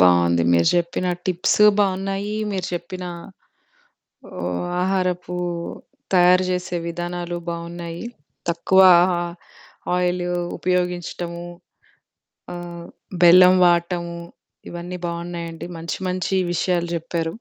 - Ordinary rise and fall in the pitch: No, narrow, 1.2 semitones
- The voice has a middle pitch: Yes, medium, 175 Hz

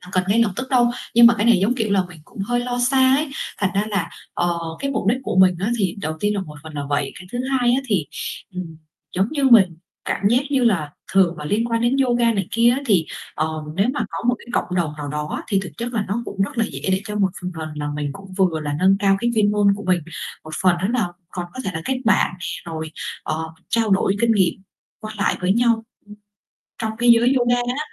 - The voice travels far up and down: No, average, 4.9 semitones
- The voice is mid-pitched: No, high, 205 Hz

